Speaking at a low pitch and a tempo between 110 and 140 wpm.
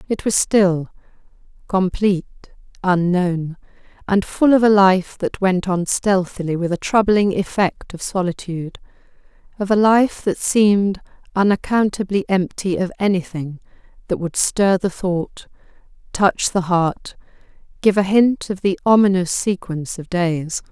No: high, 190 Hz; slow, 135 wpm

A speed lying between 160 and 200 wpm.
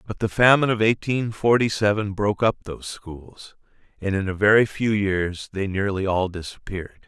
Yes: average, 180 wpm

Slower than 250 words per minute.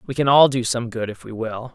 No: fast, 310 wpm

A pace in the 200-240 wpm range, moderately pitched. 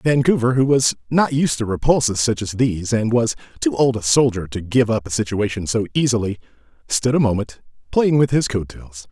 No: fast, 205 wpm; low, 115 Hz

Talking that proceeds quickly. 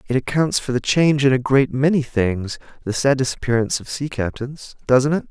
No: average, 180 wpm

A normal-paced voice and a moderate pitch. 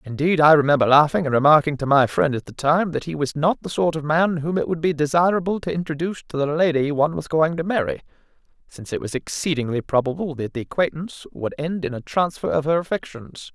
No: fast, 225 wpm; medium, 150 Hz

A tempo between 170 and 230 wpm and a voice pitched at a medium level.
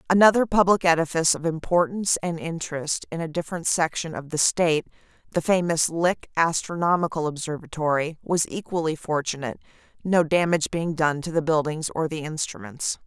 No: average, 145 wpm; medium, 165 Hz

